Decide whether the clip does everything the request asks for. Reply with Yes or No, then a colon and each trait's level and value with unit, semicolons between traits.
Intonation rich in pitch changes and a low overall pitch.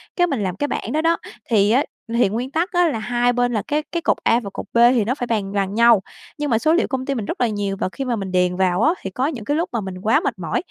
No: wide, 5.9 semitones; high, 235 Hz